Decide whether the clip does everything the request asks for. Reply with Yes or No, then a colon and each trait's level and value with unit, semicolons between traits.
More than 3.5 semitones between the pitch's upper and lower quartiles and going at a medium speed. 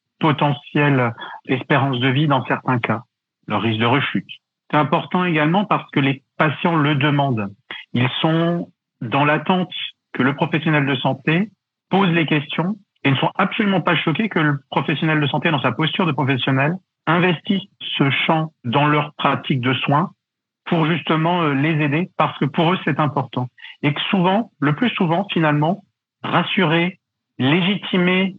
Yes: average, 4.0 semitones; average, 160 wpm